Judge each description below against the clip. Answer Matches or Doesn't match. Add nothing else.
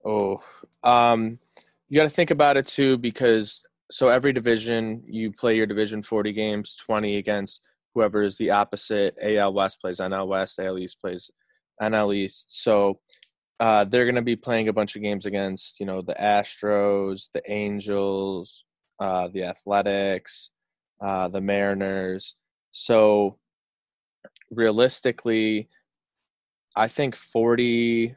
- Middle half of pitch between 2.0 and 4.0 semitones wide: Matches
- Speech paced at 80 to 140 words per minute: Matches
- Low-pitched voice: Matches